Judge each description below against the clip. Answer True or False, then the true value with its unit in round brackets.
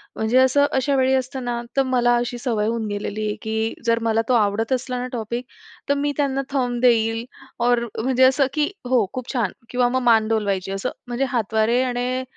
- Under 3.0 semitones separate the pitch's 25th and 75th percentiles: True (2.6 semitones)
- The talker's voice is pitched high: True (245 Hz)